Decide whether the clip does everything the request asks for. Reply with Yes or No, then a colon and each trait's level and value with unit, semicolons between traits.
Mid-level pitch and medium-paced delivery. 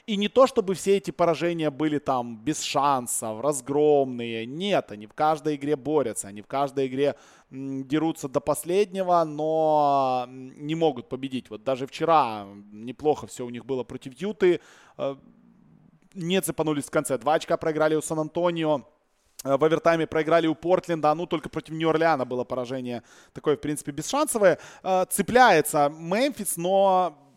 Yes: medium, 150 Hz; average, 145 wpm